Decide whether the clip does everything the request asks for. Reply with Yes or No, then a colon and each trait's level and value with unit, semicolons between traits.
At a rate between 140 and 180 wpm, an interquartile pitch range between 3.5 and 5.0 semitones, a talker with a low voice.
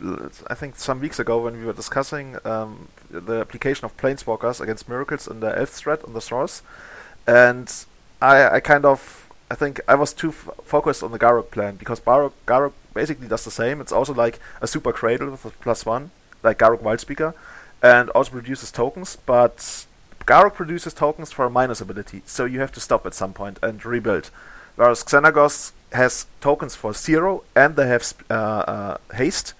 No: average, 190 wpm; average, 4.0 semitones; low, 125 Hz